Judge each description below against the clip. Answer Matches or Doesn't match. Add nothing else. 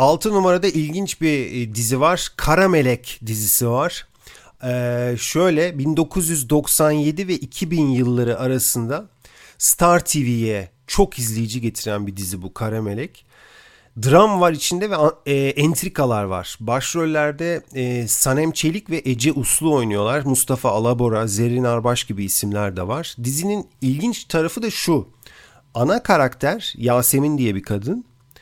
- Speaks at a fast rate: Doesn't match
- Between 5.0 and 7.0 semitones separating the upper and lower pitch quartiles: Matches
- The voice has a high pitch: Doesn't match